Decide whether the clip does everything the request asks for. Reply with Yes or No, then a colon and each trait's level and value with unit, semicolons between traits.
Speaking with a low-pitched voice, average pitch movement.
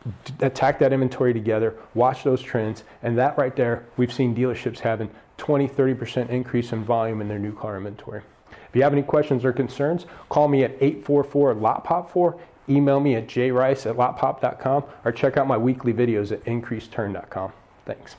Yes: low, 125 Hz; average, 3.5 semitones